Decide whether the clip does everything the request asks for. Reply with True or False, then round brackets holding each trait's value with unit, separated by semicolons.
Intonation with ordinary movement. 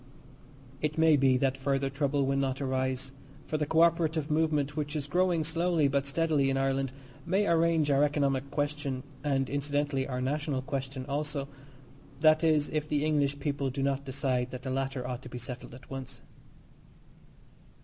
False (2.2 semitones)